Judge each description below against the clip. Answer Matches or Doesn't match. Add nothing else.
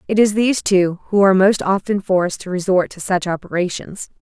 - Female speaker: Matches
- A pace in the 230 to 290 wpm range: Doesn't match